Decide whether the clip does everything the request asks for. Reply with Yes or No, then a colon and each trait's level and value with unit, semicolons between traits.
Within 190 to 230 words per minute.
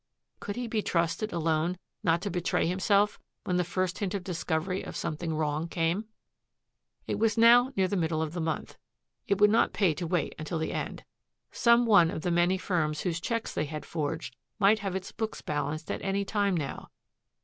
Yes: average, 195 wpm